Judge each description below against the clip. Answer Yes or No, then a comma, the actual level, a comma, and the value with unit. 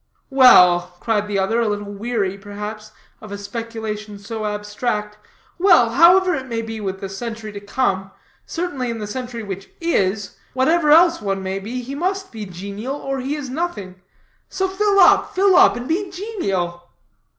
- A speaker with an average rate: Yes, average, 175 wpm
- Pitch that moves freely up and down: Yes, wide, 5.7 semitones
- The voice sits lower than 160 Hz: No, high, 225 Hz